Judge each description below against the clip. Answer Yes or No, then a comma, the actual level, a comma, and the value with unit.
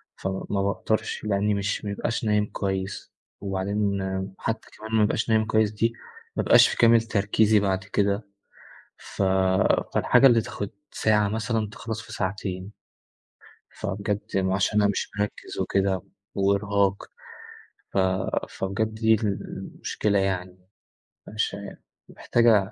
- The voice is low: Yes, low, 105 Hz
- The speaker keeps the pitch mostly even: Yes, narrow, 1.9 semitones